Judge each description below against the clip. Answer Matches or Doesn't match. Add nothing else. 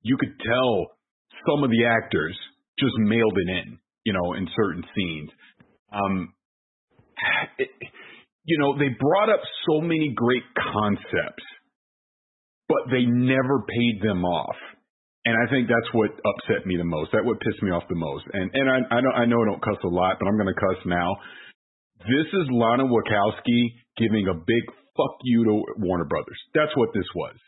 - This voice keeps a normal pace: Matches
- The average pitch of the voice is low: Matches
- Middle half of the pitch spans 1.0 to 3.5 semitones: Doesn't match